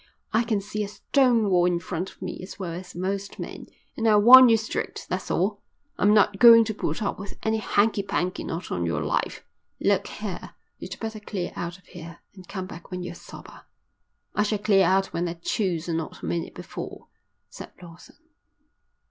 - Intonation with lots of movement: No, average, 3.4 semitones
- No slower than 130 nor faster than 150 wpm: No, average, 200 wpm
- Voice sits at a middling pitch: No, high, 195 Hz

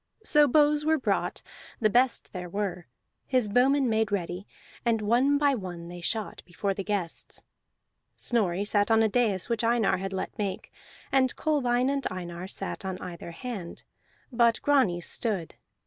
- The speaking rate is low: No, average, 160 wpm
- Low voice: No, high, 215 Hz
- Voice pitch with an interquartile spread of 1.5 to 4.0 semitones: No, average, 5.2 semitones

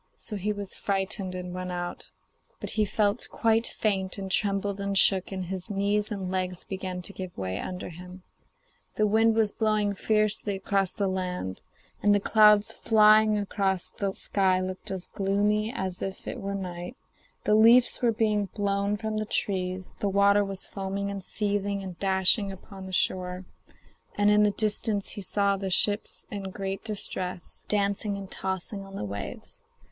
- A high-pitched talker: Yes, high, 200 Hz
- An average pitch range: No, narrow, 1.9 semitones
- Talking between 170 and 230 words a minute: Yes, average, 175 wpm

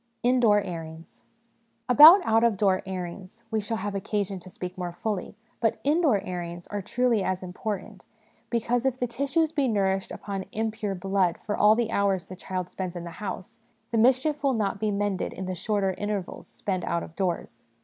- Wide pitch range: No, average, 3.7 semitones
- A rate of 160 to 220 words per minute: Yes, average, 190 wpm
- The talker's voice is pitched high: Yes, high, 205 Hz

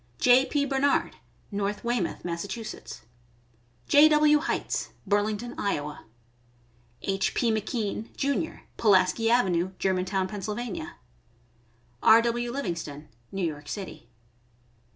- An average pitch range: No, wide, 5.8 semitones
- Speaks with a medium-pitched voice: No, high, 205 Hz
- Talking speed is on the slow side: Yes, slow, 105 wpm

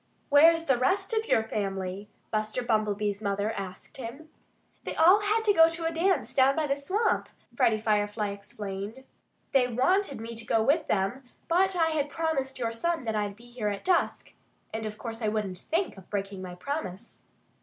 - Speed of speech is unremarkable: Yes, average, 185 wpm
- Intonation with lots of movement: Yes, wide, 7.5 semitones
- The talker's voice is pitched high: Yes, high, 235 Hz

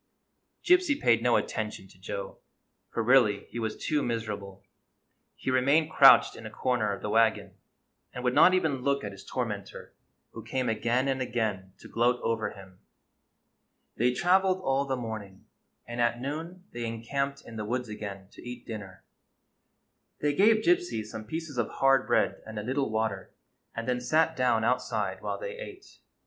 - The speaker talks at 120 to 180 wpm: Yes, average, 170 wpm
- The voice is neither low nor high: No, low, 120 Hz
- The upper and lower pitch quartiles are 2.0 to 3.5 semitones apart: No, average, 4.1 semitones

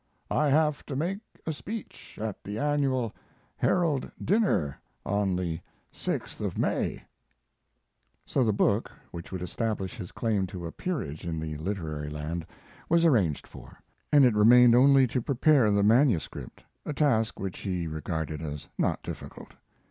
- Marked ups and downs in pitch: Yes, wide, 8.3 semitones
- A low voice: Yes, low, 110 Hz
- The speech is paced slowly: No, average, 150 wpm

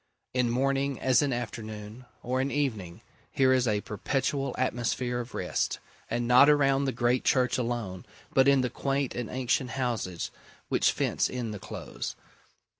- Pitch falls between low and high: No, low, 125 Hz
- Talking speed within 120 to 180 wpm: Yes, average, 160 wpm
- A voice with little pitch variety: Yes, narrow, 2.3 semitones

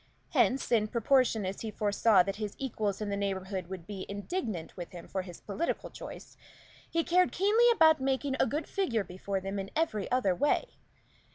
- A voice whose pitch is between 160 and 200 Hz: No, high, 210 Hz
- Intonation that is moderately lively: No, wide, 6.1 semitones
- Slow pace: No, average, 180 wpm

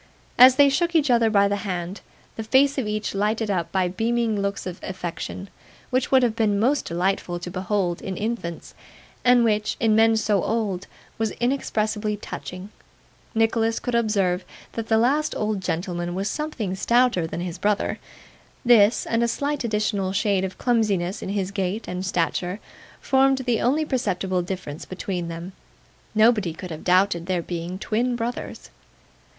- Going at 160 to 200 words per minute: Yes, average, 165 wpm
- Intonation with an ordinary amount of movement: Yes, average, 4.2 semitones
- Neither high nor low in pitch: No, high, 210 Hz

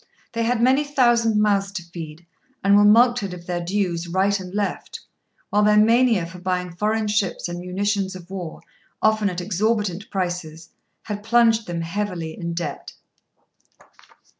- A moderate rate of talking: Yes, average, 155 wpm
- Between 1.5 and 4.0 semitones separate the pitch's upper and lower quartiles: Yes, average, 3.5 semitones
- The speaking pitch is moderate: No, high, 200 Hz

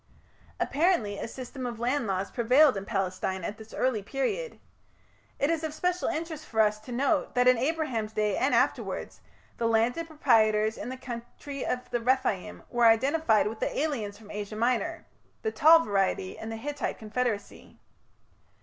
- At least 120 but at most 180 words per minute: Yes, average, 165 wpm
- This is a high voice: Yes, high, 240 Hz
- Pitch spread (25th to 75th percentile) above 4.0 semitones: Yes, average, 5.1 semitones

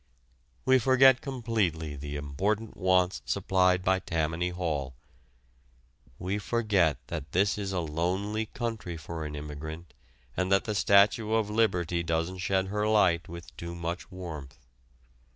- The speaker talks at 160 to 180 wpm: No, slow, 135 wpm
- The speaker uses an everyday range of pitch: Yes, average, 4.3 semitones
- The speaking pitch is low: Yes, very low, 90 Hz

